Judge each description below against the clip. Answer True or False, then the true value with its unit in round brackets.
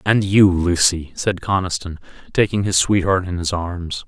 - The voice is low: True (90 Hz)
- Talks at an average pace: True (160 wpm)